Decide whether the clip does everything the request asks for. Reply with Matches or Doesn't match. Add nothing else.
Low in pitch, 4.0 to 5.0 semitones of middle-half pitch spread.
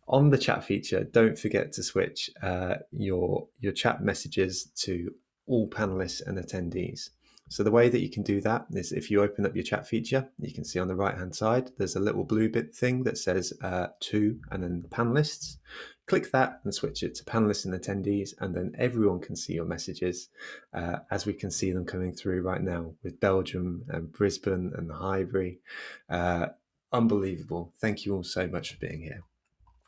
Doesn't match